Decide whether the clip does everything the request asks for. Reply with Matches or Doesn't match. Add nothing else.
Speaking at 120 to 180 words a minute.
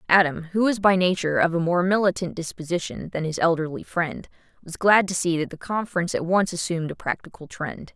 Doesn't match